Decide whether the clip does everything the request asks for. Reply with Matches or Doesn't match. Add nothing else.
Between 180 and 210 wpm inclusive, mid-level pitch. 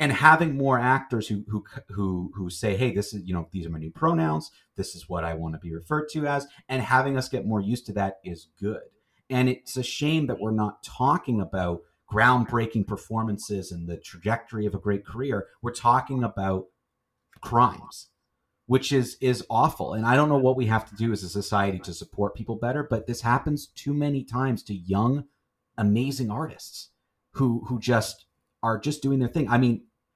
Doesn't match